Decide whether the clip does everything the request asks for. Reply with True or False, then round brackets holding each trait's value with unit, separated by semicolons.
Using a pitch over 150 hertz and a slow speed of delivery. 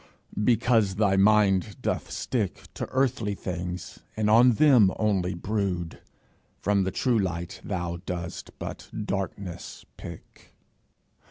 False (100 Hz; 115 wpm)